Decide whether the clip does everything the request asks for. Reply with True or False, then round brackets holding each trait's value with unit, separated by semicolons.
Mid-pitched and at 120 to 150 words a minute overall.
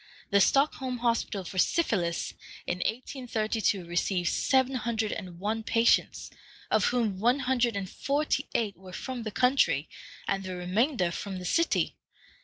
False (220 Hz; 145 wpm)